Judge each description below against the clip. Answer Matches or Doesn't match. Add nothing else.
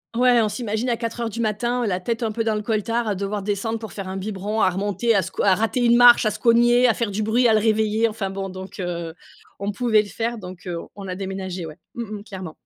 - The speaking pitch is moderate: Doesn't match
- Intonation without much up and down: Doesn't match